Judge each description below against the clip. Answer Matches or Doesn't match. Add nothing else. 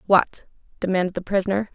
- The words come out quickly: Doesn't match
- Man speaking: Doesn't match